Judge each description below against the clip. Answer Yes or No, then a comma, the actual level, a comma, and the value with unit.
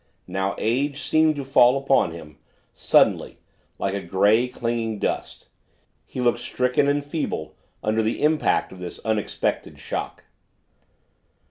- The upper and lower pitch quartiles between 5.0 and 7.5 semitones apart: Yes, wide, 5.4 semitones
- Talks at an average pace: No, slow, 130 wpm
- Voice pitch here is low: Yes, low, 120 Hz